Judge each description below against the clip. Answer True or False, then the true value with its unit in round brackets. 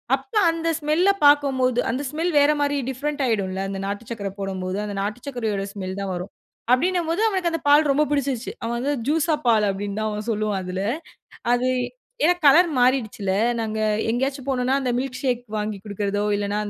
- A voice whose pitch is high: True (250 Hz)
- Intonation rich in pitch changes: True (5.9 semitones)